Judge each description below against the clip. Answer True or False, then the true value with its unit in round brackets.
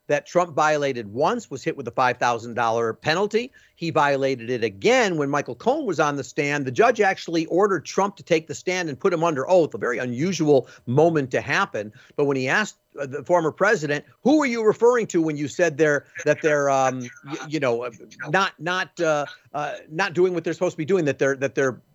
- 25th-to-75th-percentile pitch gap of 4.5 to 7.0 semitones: True (4.8 semitones)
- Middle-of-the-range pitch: True (155 Hz)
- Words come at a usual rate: False (220 wpm)